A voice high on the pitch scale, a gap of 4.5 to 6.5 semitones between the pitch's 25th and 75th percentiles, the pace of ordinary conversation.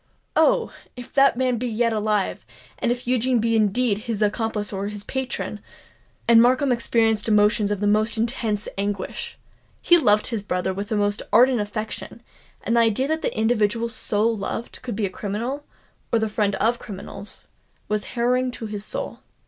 No: high, 225 Hz; average, 2.7 semitones; average, 175 wpm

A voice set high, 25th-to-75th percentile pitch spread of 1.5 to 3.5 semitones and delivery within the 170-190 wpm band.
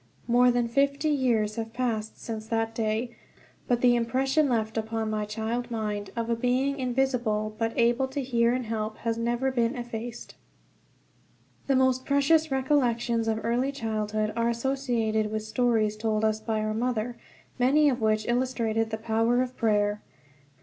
No: high, 235 Hz; narrow, 2.5 semitones; average, 160 wpm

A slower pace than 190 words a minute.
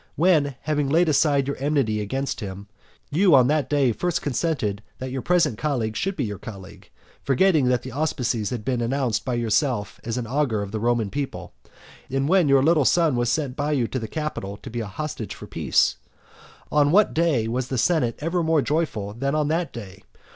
No: average, 200 wpm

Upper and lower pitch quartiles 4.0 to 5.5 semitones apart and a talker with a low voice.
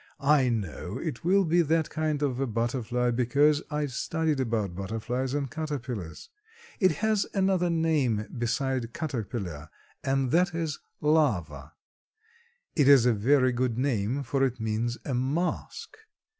Yes: average, 4.7 semitones; low, 130 Hz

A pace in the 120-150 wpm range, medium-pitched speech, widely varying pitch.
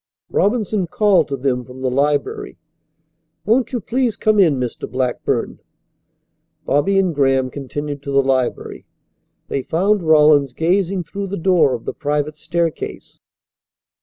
Yes: slow, 135 wpm; medium, 155 Hz; wide, 6.3 semitones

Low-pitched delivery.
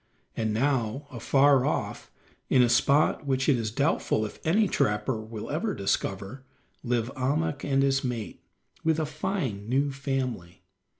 Yes: low, 130 Hz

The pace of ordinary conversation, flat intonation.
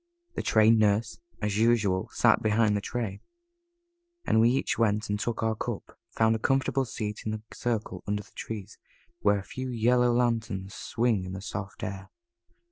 Yes: average, 175 wpm; narrow, 2.2 semitones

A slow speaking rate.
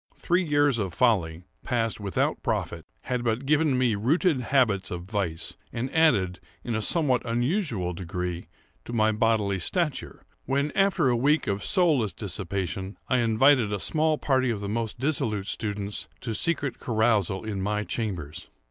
No: average, 160 wpm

